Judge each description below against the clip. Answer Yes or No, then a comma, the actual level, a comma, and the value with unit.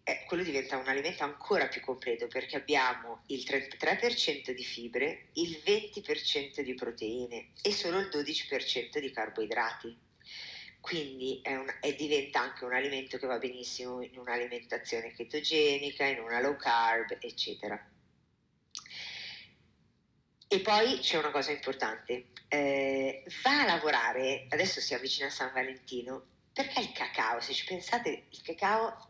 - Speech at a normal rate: Yes, average, 135 wpm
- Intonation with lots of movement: Yes, wide, 5.8 semitones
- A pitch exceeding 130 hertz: Yes, medium, 140 Hz